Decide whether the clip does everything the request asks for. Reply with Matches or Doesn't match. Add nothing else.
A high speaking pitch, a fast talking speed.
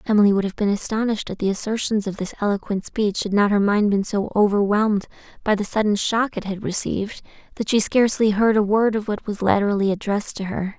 Matches